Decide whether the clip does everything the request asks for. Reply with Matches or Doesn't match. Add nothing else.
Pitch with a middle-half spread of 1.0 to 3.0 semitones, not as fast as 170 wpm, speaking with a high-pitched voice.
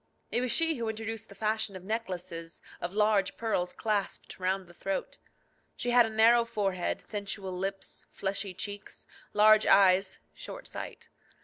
Matches